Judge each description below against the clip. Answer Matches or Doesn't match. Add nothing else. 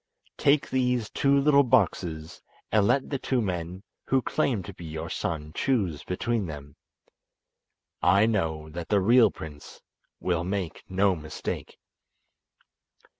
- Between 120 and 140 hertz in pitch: Doesn't match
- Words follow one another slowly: Matches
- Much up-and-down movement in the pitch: Matches